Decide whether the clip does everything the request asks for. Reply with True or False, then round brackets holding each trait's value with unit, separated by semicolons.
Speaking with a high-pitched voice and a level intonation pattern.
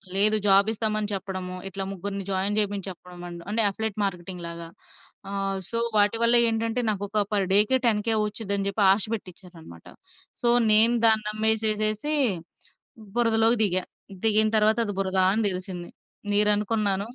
True (205 Hz; 2.3 semitones)